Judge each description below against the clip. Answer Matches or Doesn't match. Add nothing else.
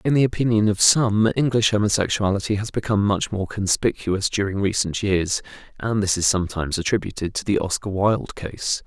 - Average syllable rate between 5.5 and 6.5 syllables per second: Matches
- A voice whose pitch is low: Matches